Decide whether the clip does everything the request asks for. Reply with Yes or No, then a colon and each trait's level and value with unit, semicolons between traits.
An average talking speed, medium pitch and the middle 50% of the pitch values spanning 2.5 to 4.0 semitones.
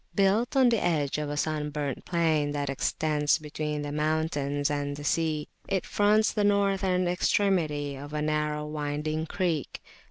Yes: average, 155 wpm; medium, 155 Hz; average, 3.6 semitones